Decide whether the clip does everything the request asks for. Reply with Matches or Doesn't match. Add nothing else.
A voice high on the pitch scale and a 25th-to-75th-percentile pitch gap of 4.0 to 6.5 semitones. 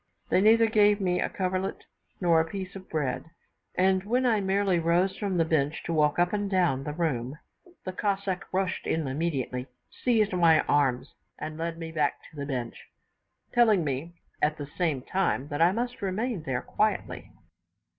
Doesn't match